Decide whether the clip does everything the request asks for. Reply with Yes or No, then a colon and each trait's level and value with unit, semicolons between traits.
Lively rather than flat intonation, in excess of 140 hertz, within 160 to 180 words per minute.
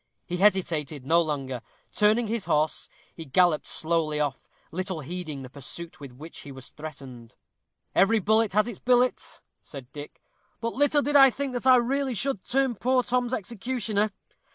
Yes: wide, 8.2 semitones; high, 190 Hz; average, 165 wpm